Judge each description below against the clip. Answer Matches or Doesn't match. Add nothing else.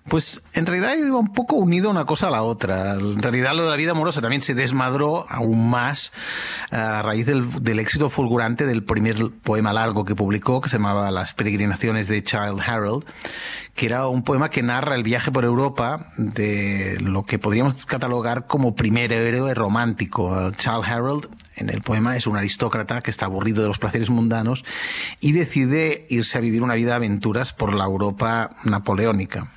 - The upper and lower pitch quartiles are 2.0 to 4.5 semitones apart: Matches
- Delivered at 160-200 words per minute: Matches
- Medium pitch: Doesn't match